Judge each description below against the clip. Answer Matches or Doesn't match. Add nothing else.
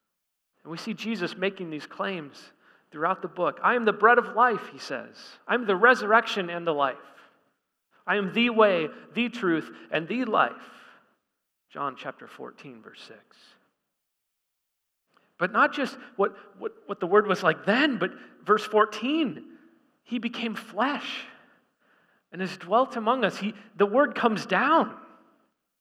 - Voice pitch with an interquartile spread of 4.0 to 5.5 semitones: Matches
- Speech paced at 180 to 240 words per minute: Doesn't match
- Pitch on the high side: Matches